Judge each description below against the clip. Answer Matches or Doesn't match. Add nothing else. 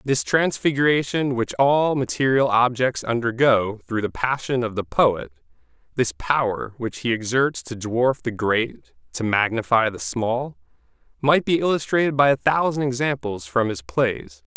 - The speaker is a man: Matches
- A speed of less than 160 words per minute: Matches